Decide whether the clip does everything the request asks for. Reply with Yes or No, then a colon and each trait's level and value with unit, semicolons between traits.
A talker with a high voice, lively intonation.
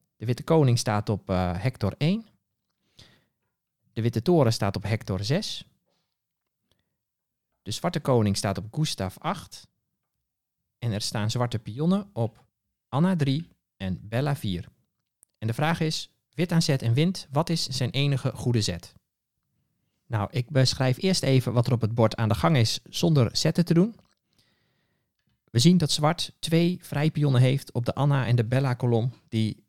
No: low, 130 Hz; wide, 5.8 semitones